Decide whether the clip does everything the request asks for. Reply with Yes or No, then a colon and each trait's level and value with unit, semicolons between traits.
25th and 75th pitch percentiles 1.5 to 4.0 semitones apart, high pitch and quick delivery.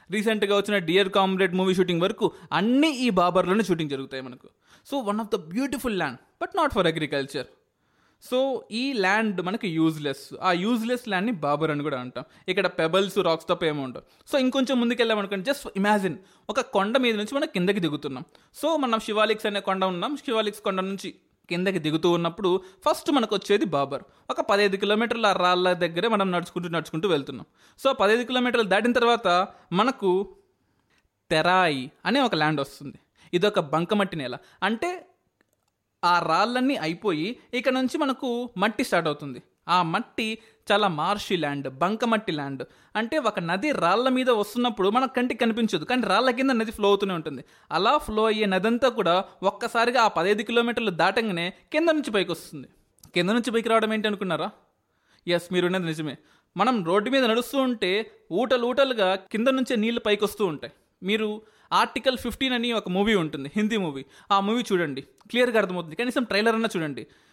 No: average, 5.1 semitones; high, 205 Hz; fast, 165 wpm